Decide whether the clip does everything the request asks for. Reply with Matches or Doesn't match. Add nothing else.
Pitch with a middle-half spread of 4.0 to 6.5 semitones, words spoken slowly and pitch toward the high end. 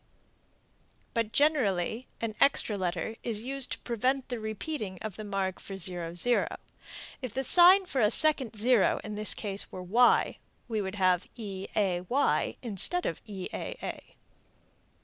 Matches